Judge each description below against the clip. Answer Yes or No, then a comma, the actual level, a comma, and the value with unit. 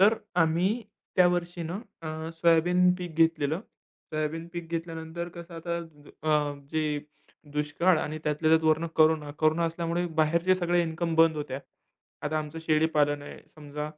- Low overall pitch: No, medium, 160 Hz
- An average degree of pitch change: No, narrow, 1.8 semitones